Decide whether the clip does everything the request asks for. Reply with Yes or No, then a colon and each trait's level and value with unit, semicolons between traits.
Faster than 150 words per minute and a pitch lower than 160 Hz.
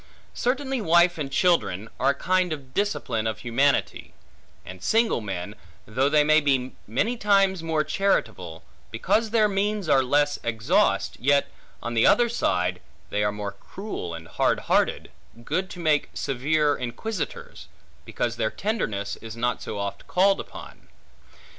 No: average, 145 wpm; medium, 140 Hz